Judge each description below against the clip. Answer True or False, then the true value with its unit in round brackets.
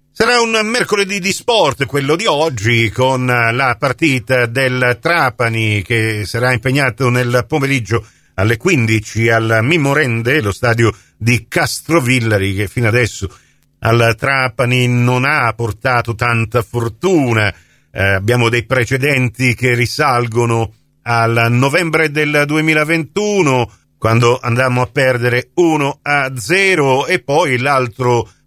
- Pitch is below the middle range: True (125 Hz)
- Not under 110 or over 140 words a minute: True (115 wpm)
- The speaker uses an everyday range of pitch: True (3.4 semitones)